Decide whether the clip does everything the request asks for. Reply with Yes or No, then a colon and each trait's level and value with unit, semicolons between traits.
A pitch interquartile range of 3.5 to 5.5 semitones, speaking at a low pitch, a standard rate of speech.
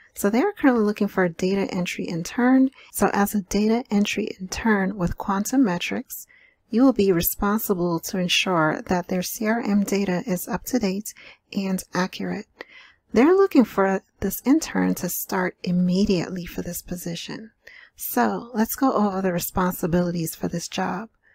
No: average, 3.8 semitones; high, 195 Hz; average, 155 wpm